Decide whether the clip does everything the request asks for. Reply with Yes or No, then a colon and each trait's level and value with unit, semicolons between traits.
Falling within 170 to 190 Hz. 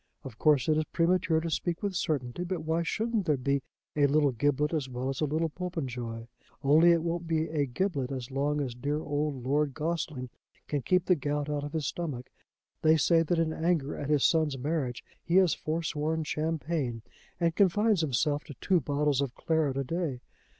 No: medium, 150 Hz